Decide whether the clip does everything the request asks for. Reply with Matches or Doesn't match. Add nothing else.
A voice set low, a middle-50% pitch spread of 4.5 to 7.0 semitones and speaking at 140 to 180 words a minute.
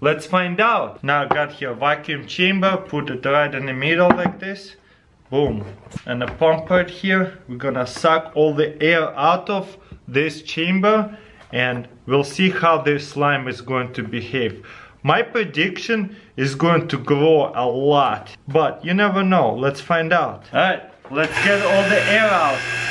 Doesn't match